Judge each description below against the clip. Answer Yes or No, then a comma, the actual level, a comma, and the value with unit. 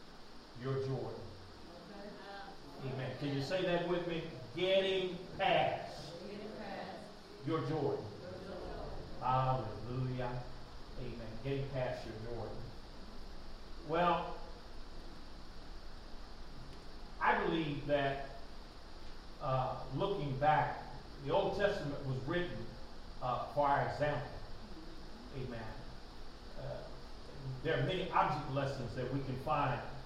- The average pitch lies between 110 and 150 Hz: Yes, medium, 140 Hz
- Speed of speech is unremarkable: No, slow, 90 wpm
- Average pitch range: Yes, average, 5.0 semitones